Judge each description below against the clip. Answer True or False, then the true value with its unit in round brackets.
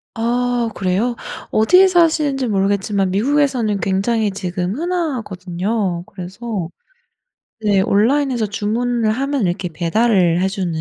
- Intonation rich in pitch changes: False (4.5 semitones)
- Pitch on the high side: True (215 Hz)